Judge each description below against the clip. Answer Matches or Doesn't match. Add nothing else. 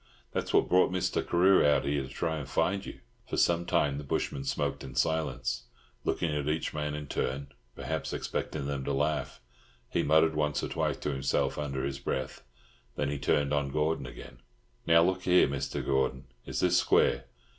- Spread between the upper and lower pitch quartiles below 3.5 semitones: Matches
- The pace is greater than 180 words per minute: Matches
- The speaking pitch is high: Doesn't match